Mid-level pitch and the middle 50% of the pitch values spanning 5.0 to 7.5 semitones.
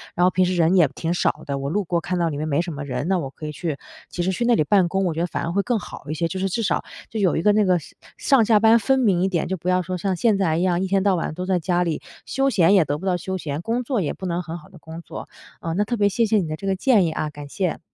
No: medium, 180 Hz; average, 3.3 semitones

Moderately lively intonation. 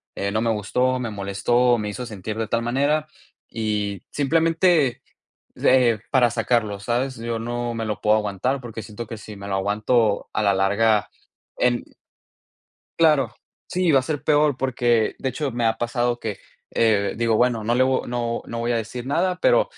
Yes: average, 3.2 semitones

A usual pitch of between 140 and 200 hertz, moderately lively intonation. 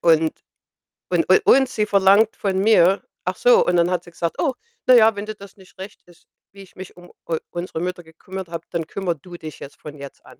Yes: medium, 185 Hz; average, 3.1 semitones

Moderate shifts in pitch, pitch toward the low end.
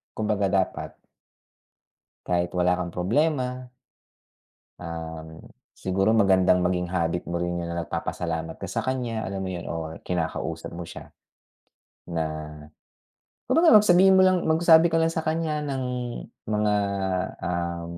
No: wide, 7.2 semitones; very low, 95 Hz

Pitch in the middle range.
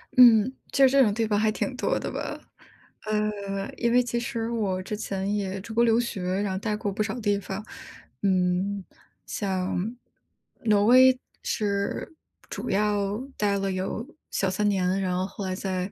No: high, 205 Hz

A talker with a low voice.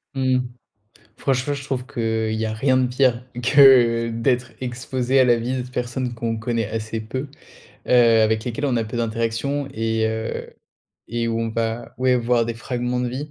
Yes: low, 120 Hz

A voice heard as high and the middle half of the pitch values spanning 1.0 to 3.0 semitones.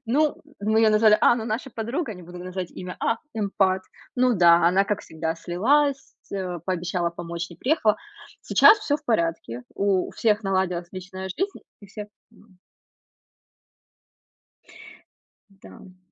No: high, 195 Hz; average, 4.0 semitones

